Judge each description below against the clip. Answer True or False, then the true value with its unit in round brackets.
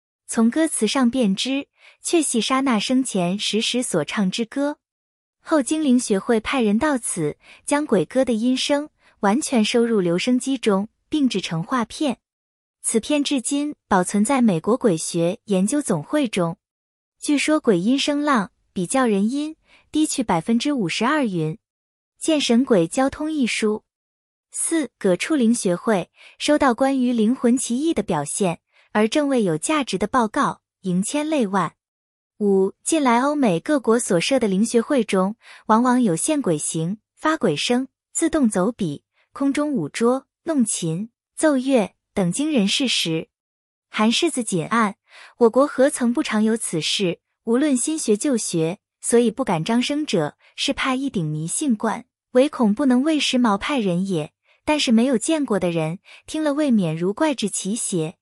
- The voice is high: True (235 Hz)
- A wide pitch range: True (5.9 semitones)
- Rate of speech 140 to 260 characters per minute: True (225 characters per minute)